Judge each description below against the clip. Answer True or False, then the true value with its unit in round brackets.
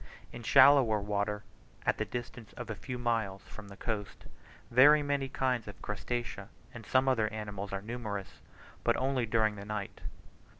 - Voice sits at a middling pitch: False (115 Hz)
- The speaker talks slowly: False (165 wpm)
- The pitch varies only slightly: False (3.5 semitones)